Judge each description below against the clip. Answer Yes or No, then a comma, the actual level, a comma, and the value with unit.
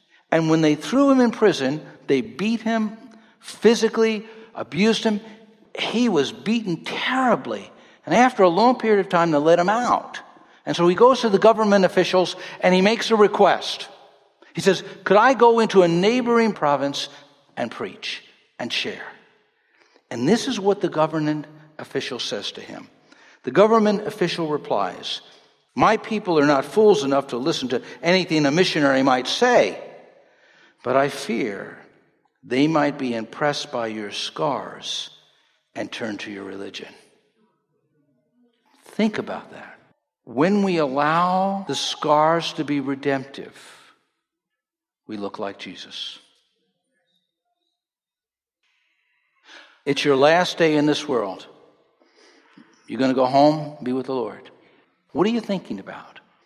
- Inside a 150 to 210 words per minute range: No, average, 140 wpm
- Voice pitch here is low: No, medium, 180 Hz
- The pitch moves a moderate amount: No, wide, 7.3 semitones